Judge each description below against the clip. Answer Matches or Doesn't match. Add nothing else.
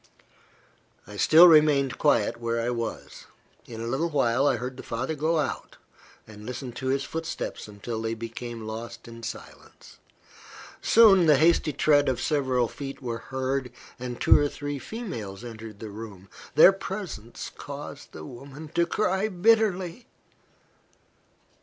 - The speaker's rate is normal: Matches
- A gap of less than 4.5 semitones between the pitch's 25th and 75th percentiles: Doesn't match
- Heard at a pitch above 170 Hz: Doesn't match